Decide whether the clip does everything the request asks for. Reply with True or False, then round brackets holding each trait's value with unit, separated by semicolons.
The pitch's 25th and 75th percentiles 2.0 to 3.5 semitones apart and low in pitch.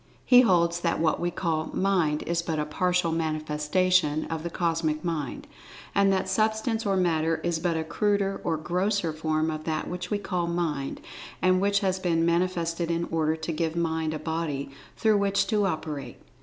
False (2.7 semitones; 170 Hz)